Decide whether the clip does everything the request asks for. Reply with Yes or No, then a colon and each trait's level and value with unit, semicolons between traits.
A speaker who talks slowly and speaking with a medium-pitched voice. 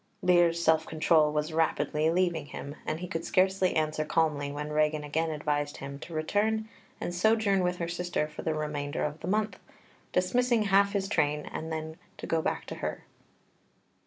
No: average, 180 wpm; medium, 160 Hz